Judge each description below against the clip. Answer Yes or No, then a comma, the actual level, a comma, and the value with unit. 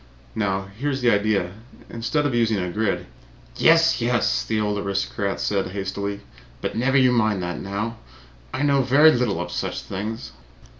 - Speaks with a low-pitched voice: Yes, low, 110 Hz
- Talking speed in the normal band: Yes, average, 165 wpm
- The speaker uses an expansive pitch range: No, average, 4.0 semitones